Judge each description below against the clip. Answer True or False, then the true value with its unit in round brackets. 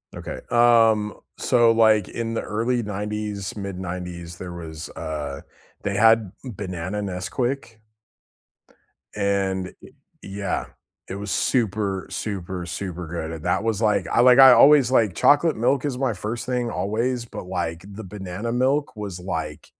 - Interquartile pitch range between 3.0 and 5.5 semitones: True (4.3 semitones)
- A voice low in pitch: True (105 Hz)